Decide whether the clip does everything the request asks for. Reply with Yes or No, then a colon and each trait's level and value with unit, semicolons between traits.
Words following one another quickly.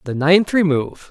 No: average, 165 wpm